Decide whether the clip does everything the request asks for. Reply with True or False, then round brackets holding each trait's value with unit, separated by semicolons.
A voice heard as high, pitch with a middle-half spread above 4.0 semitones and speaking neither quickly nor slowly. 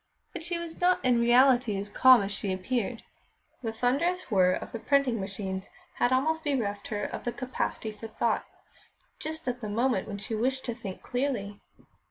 True (240 Hz; 4.4 semitones; 185 wpm)